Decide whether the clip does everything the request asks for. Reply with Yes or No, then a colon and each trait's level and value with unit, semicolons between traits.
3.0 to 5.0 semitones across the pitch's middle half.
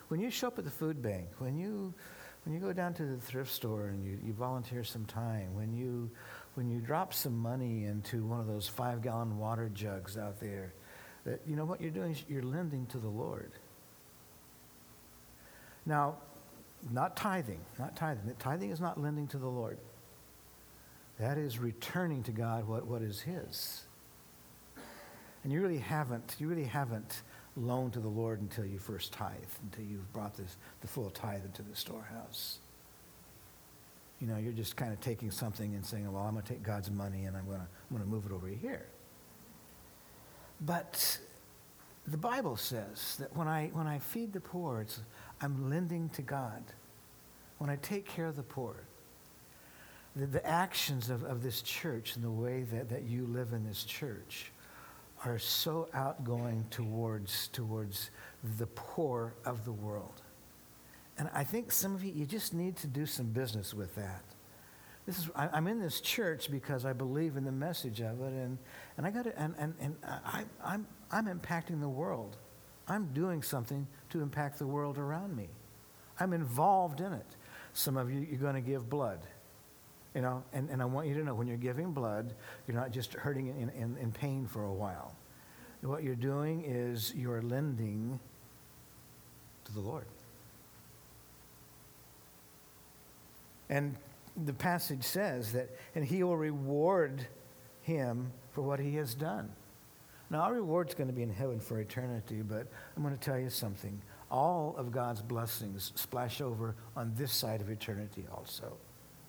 No: wide, 5.4 semitones